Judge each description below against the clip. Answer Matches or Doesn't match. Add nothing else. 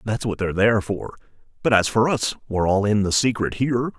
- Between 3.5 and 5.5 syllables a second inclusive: Doesn't match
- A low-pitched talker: Matches